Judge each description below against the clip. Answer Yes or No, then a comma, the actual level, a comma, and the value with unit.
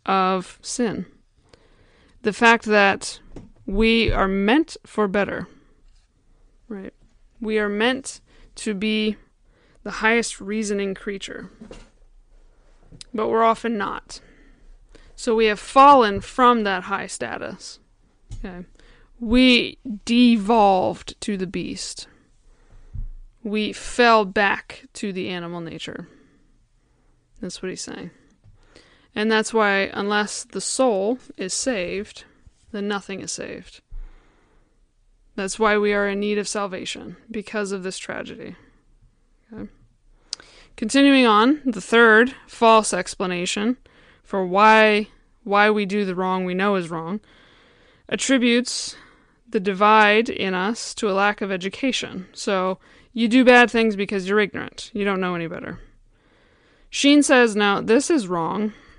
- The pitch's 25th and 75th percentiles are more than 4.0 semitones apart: No, average, 3.2 semitones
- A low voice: No, high, 210 Hz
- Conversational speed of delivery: No, slow, 120 wpm